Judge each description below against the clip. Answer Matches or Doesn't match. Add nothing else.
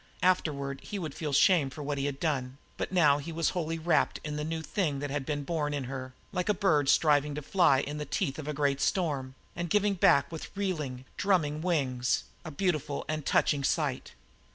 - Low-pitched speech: Doesn't match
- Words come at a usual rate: Doesn't match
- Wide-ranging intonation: Doesn't match